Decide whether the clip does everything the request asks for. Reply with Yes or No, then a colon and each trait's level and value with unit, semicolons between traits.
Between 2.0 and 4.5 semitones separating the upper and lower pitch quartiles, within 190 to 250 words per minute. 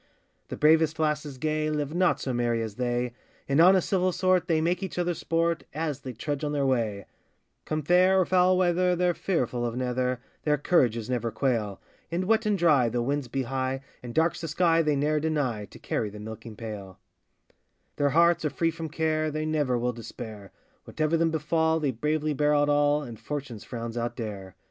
No: average, 5.2 semitones; average, 195 wpm